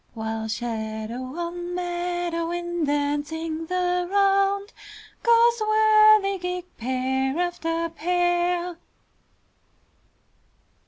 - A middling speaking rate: No, slow, 70 wpm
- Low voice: No, very high, 345 Hz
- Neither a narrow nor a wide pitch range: Yes, average, 3.7 semitones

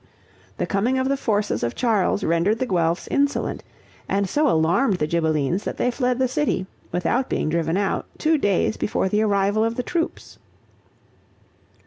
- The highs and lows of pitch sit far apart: Yes, wide, 6.4 semitones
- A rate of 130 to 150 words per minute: No, average, 165 wpm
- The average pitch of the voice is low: No, high, 205 Hz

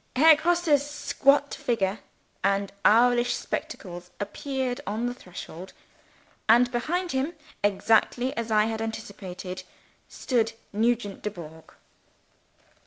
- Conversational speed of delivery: No, slow, 105 wpm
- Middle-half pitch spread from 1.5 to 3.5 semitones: No, average, 4.7 semitones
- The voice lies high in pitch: Yes, high, 230 Hz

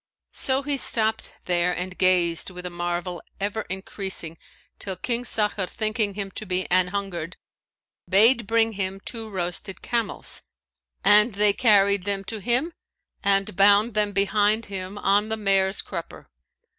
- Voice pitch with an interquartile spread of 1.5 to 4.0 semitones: Yes, average, 2.7 semitones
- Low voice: No, high, 200 Hz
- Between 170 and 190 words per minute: No, average, 145 wpm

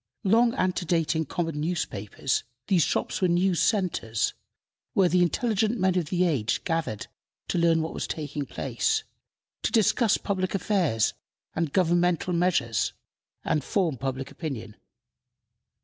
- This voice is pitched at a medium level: Yes, medium, 175 Hz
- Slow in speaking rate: Yes, slow, 130 wpm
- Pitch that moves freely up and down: No, average, 3.9 semitones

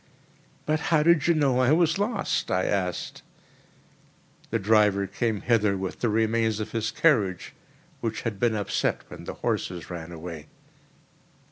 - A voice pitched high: No, low, 110 Hz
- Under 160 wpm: Yes, average, 150 wpm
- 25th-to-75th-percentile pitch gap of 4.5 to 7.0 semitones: Yes, average, 5.2 semitones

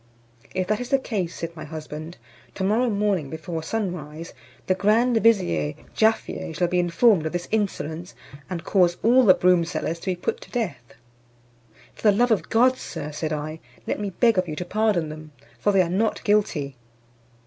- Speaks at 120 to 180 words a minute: No, average, 190 wpm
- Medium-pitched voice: Yes, medium, 180 Hz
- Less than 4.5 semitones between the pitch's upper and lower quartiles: No, average, 5.0 semitones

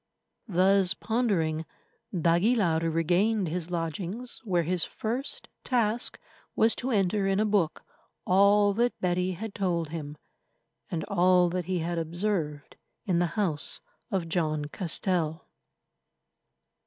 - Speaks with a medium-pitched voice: Yes, medium, 180 Hz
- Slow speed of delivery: Yes, slow, 120 wpm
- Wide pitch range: No, average, 3.7 semitones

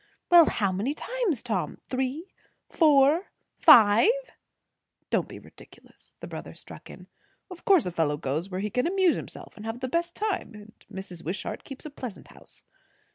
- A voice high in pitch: Yes, very high, 250 Hz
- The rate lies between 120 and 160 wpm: No, average, 170 wpm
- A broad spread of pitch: Yes, wide, 9.0 semitones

